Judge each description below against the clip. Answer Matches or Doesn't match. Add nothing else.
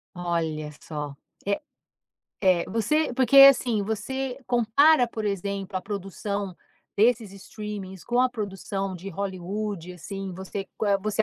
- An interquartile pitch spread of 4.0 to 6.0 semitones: Doesn't match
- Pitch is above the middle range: Matches